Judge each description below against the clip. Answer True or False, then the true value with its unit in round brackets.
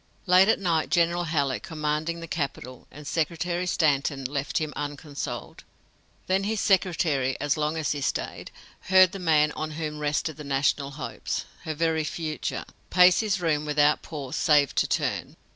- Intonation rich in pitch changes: False (2.9 semitones)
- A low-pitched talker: False (155 Hz)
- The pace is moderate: True (160 wpm)